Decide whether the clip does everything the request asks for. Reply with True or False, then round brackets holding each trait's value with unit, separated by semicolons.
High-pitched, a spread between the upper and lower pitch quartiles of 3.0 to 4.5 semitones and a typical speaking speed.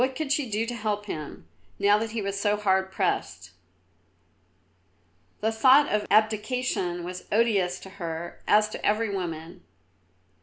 True (210 Hz; 3.5 semitones; 150 wpm)